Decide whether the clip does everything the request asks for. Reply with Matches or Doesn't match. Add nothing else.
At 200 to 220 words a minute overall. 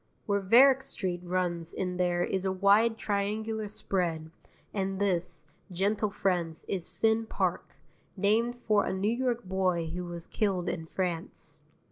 Doesn't match